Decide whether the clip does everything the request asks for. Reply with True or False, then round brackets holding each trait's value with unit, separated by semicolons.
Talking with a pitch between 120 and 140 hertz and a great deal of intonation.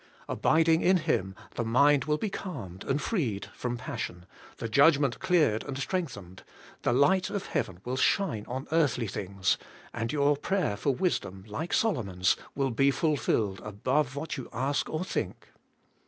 True (135 Hz; 6.6 semitones)